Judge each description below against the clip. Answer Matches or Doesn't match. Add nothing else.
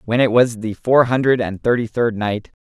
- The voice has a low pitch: Matches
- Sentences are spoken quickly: Matches